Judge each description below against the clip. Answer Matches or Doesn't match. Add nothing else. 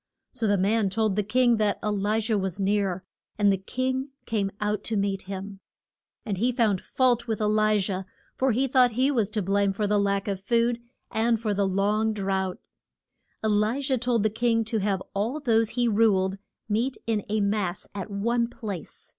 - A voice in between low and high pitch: Doesn't match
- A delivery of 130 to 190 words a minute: Doesn't match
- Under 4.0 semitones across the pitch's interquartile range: Matches